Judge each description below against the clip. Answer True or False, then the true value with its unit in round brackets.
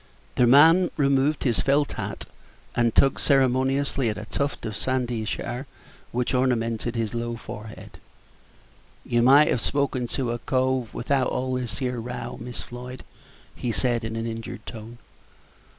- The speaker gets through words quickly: False (150 wpm)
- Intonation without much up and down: True (2.3 semitones)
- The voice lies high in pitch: False (125 Hz)